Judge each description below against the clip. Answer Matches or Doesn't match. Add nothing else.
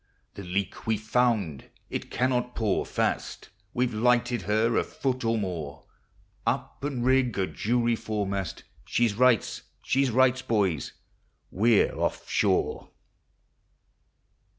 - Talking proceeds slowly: Matches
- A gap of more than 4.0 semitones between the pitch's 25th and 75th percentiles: Doesn't match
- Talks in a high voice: Doesn't match